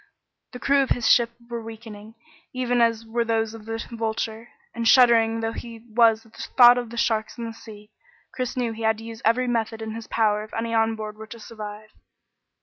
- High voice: Yes, high, 225 Hz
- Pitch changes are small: Yes, narrow, 1.1 semitones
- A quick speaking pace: Yes, fast, 220 wpm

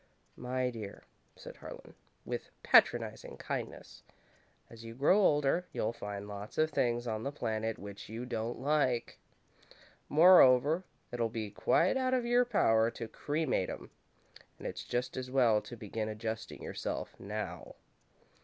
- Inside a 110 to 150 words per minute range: Yes, average, 145 wpm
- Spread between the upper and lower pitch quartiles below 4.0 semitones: No, average, 4.9 semitones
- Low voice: Yes, low, 120 Hz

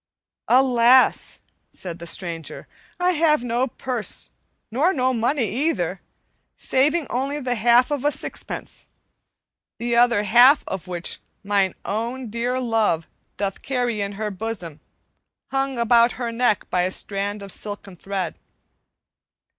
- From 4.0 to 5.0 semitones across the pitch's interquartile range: Yes, average, 4.3 semitones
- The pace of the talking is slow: Yes, slow, 130 wpm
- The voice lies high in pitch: Yes, high, 235 Hz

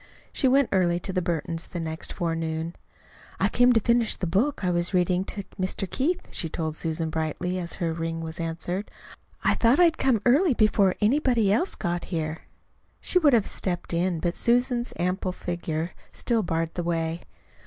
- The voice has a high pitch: No, medium, 180 Hz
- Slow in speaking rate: No, average, 180 wpm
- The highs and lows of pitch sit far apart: Yes, wide, 5.8 semitones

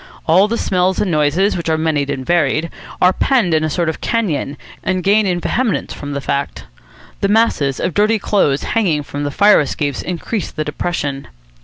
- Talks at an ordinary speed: Yes, average, 195 wpm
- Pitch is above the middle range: No, medium, 170 Hz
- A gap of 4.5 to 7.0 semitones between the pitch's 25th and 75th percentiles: Yes, wide, 5.4 semitones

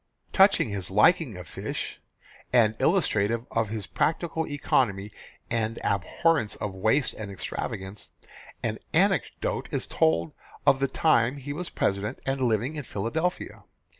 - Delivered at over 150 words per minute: No, slow, 135 wpm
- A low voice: Yes, low, 115 Hz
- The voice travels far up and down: Yes, wide, 6.0 semitones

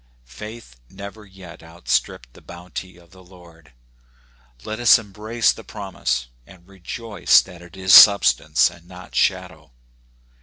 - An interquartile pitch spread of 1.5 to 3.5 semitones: Yes, average, 3.1 semitones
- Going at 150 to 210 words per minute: No, average, 140 wpm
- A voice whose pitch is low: Yes, very low, 95 Hz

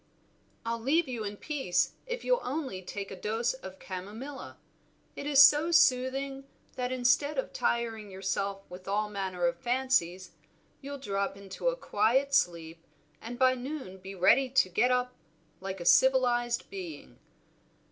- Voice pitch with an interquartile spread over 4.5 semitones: Yes, wide, 5.6 semitones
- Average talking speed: Yes, average, 150 wpm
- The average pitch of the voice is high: Yes, high, 235 Hz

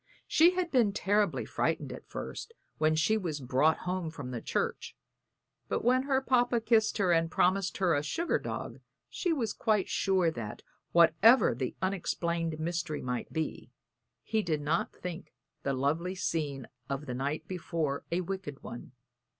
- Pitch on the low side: No, medium, 170 Hz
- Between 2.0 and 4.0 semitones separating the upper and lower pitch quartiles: No, wide, 5.5 semitones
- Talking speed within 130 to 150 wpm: No, average, 160 wpm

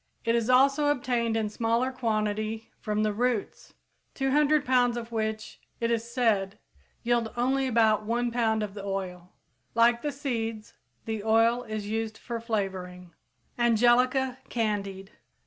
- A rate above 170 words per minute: No, average, 140 wpm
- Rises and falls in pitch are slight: Yes, narrow, 2.3 semitones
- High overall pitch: Yes, high, 230 Hz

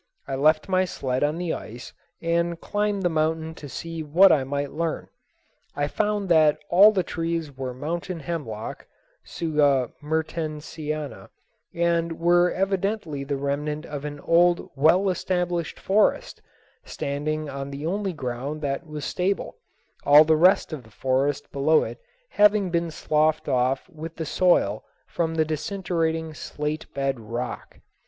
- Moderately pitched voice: Yes, medium, 155 Hz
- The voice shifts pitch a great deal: No, average, 3.2 semitones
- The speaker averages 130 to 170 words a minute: Yes, average, 145 wpm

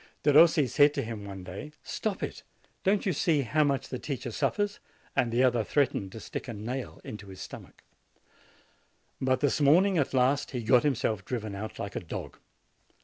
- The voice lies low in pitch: Yes, low, 130 Hz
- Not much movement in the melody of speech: No, average, 5.2 semitones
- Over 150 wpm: Yes, average, 185 wpm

